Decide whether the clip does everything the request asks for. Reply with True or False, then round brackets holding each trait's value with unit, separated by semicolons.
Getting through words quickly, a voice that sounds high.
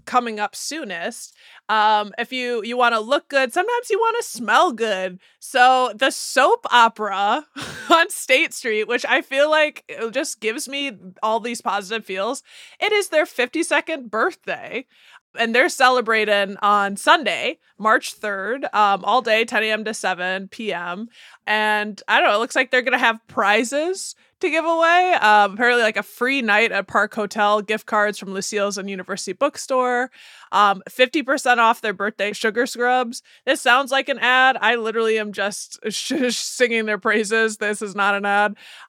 False (170 wpm; 230 Hz)